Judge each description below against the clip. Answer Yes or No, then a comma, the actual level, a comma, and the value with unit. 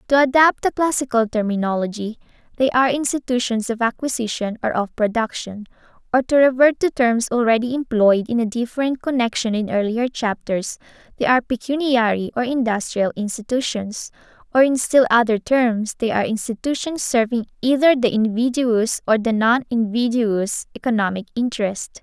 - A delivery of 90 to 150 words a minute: Yes, average, 140 wpm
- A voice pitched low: No, high, 235 Hz